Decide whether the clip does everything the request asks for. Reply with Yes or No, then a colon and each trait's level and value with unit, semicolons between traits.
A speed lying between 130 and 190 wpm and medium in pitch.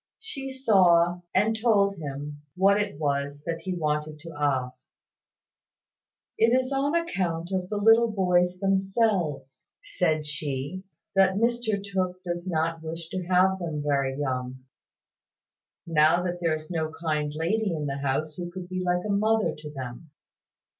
Yes: average, 155 wpm; medium, 175 Hz